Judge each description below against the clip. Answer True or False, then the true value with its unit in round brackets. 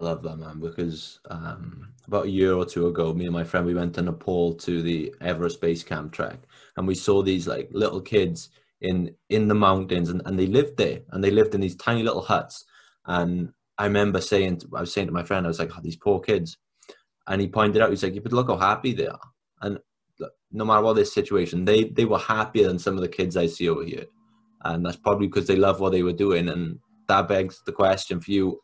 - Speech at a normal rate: False (245 wpm)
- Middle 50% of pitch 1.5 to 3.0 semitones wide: True (2.6 semitones)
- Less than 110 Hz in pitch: True (95 Hz)